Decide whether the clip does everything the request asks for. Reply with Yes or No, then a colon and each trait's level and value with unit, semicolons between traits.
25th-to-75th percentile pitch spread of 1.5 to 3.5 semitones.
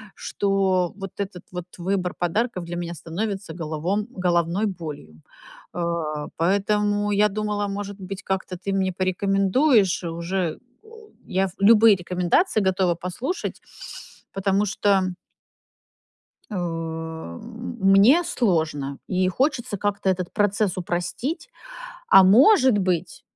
Yes: average, 2.9 semitones